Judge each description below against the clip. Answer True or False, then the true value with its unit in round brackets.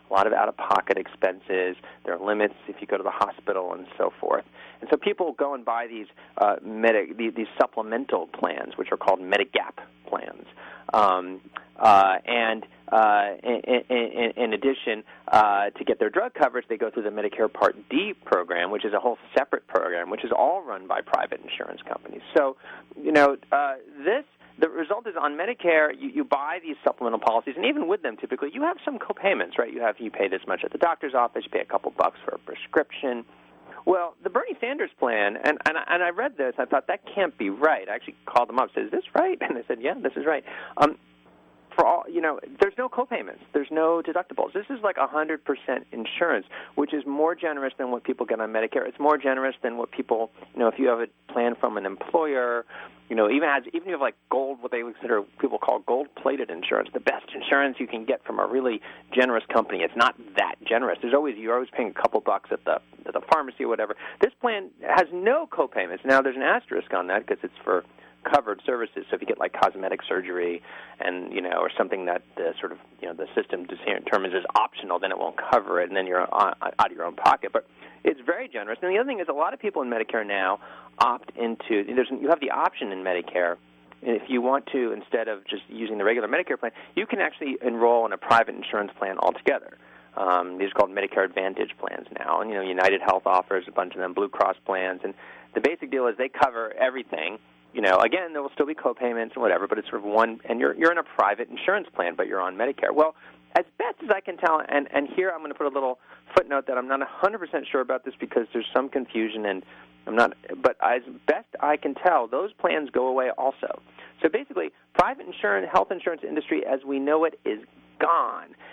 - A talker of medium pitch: False (130 Hz)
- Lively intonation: True (6.1 semitones)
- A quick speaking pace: True (230 wpm)